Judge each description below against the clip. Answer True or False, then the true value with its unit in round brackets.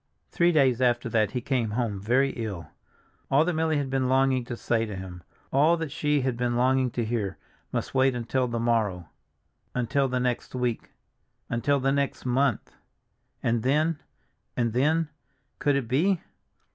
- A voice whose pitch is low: True (125 Hz)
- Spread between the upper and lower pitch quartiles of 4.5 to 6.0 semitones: False (2.9 semitones)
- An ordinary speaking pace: True (160 wpm)